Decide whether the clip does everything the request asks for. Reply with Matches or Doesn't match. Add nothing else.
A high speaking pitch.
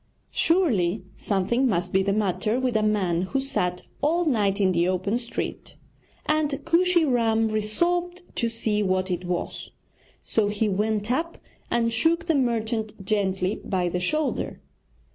Matches